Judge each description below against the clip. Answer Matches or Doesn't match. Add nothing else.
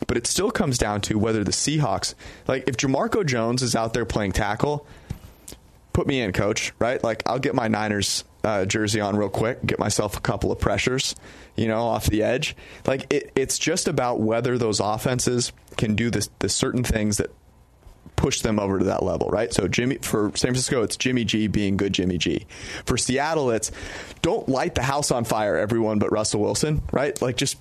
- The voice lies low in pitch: Matches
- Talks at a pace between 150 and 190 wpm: Doesn't match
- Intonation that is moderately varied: Matches